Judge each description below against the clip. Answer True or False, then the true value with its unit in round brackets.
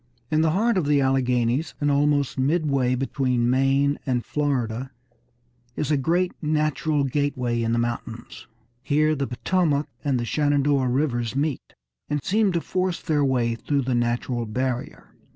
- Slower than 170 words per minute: True (150 wpm)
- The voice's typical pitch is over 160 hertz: False (140 Hz)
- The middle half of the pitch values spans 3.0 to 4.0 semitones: True (3.4 semitones)